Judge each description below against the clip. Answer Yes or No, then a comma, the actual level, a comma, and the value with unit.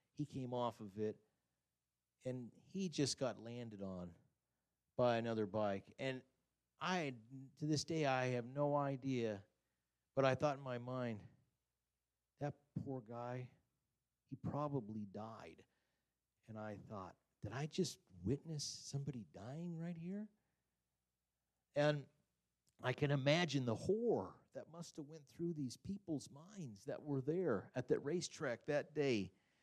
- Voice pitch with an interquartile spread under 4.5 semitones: No, wide, 5.6 semitones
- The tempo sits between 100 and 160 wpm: Yes, average, 140 wpm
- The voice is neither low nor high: No, low, 130 Hz